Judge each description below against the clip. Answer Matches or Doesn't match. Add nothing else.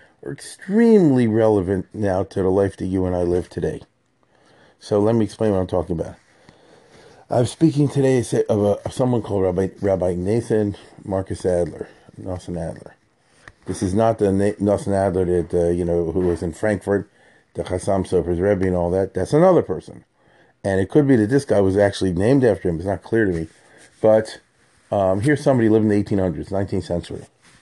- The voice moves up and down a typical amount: Matches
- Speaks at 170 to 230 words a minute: Matches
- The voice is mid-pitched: Doesn't match